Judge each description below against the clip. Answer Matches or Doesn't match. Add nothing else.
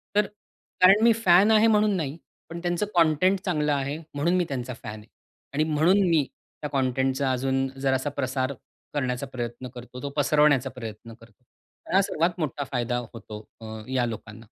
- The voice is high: Doesn't match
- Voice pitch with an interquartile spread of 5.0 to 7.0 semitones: Matches